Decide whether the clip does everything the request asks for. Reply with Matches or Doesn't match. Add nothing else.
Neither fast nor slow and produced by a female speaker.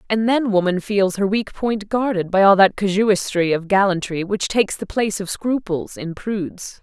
Matches